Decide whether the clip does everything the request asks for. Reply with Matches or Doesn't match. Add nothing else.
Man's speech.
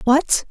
Doesn't match